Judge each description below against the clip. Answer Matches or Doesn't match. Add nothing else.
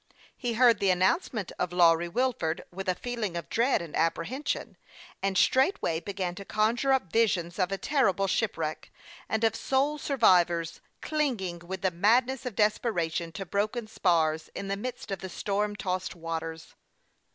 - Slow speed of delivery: Doesn't match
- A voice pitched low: Doesn't match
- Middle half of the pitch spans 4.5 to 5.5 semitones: Matches